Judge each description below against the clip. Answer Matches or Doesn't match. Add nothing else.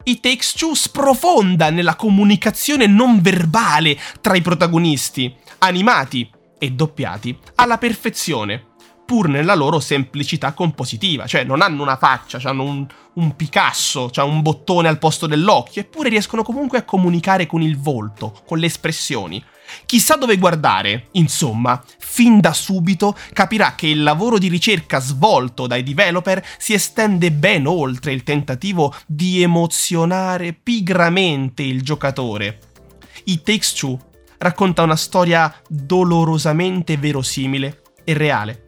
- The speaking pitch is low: Doesn't match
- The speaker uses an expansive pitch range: Matches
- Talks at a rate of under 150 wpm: Matches